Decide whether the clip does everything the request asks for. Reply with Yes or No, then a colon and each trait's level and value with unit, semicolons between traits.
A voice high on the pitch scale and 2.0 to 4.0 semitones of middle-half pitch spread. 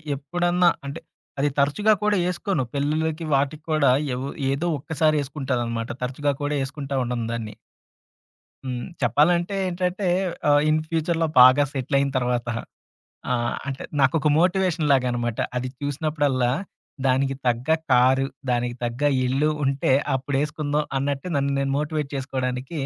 No: medium, 140 Hz; average, 3.4 semitones